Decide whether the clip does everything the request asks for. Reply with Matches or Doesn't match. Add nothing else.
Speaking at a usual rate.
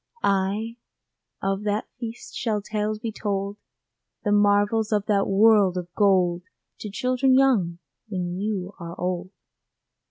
Doesn't match